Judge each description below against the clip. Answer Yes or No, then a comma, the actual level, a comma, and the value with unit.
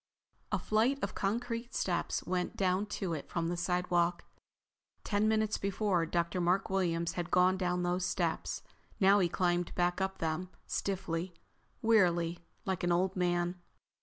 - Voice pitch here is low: No, medium, 180 Hz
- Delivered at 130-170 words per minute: Yes, average, 150 wpm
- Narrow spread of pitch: Yes, narrow, 2.0 semitones